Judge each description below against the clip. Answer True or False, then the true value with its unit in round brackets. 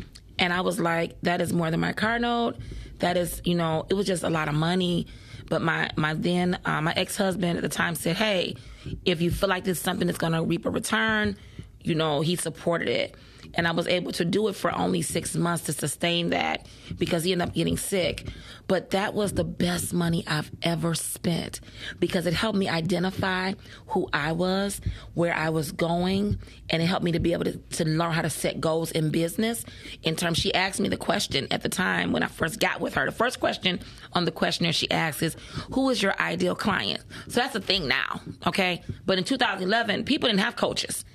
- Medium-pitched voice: True (175 Hz)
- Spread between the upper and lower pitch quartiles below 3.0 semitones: True (2.5 semitones)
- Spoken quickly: True (220 wpm)